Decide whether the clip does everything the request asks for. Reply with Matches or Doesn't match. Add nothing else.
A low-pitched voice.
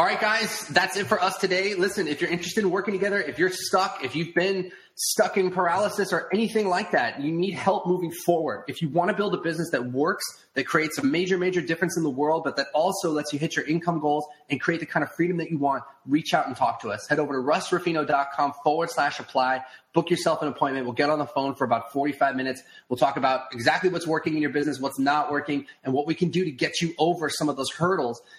Doesn't match